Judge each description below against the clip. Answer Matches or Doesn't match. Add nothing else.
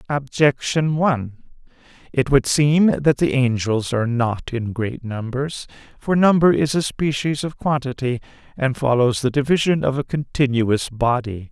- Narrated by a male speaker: Matches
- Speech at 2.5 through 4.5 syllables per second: Matches